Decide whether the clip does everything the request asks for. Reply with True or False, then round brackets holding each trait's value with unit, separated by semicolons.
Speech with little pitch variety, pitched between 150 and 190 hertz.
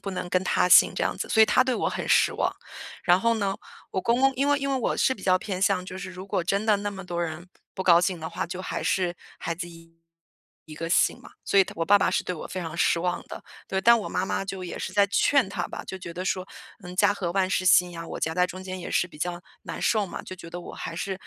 True (2.3 semitones; 185 Hz)